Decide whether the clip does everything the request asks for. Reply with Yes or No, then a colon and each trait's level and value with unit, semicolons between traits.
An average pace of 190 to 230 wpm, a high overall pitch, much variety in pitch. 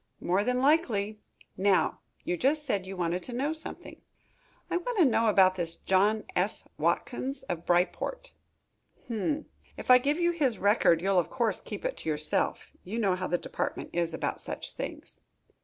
No: average, 175 wpm; high, 215 Hz; wide, 6.9 semitones